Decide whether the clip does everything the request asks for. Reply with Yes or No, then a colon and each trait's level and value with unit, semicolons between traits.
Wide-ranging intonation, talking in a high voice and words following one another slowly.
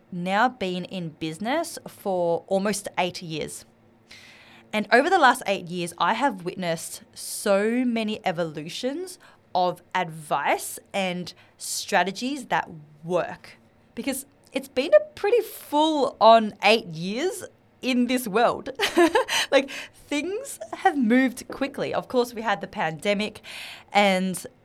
Yes: wide, 7.2 semitones; high, 210 Hz; slow, 120 wpm